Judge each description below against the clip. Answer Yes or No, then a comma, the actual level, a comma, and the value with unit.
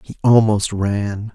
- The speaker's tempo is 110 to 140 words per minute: Yes, slow, 135 wpm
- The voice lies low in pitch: Yes, low, 105 Hz